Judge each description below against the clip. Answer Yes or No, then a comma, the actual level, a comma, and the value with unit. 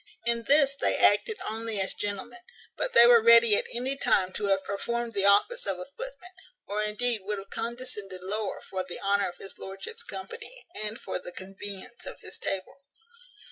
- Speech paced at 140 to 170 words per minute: No, average, 185 wpm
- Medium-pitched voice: No, high, 215 Hz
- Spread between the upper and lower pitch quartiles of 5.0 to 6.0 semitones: No, average, 3.6 semitones